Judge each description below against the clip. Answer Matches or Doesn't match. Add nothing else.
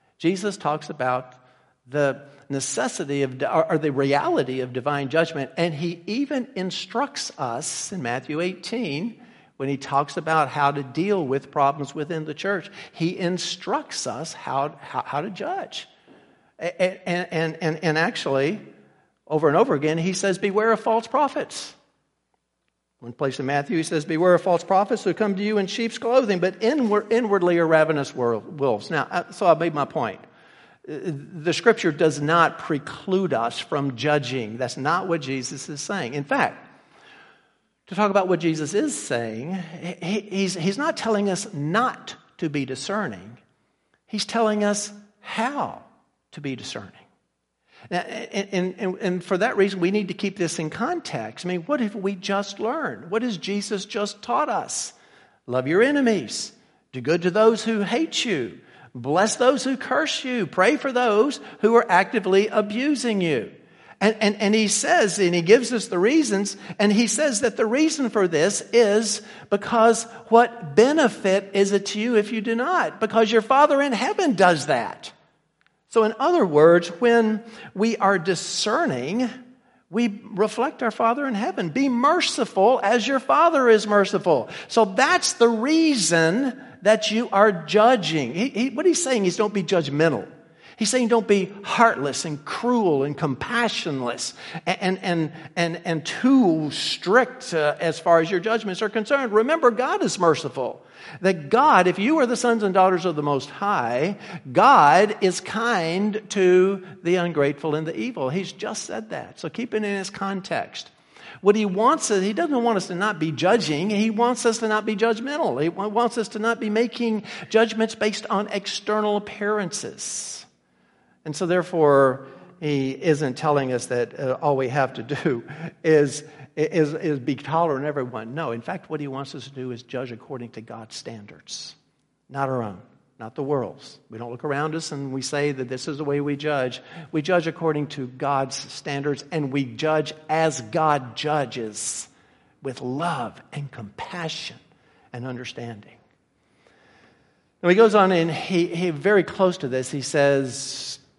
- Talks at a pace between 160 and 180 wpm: Matches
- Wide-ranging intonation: Matches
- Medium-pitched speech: Matches